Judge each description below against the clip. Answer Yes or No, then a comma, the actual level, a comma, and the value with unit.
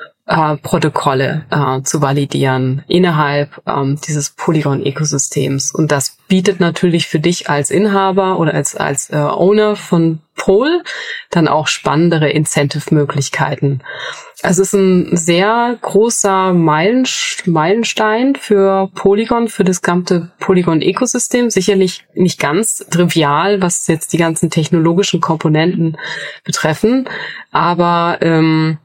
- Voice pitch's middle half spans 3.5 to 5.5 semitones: Yes, average, 4.3 semitones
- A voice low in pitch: No, medium, 170 Hz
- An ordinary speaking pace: No, slow, 115 wpm